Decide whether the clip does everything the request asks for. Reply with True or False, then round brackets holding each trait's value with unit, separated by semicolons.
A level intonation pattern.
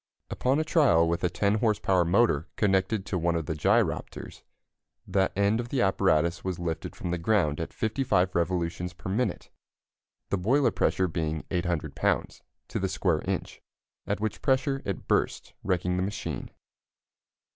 False (4.0 semitones)